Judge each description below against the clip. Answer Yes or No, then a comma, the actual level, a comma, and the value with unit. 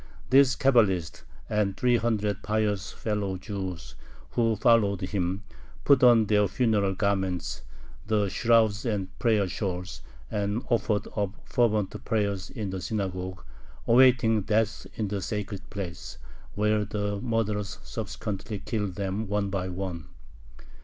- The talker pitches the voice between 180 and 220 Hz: No, low, 105 Hz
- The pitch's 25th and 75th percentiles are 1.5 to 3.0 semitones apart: Yes, narrow, 2.5 semitones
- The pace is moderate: No, slow, 125 wpm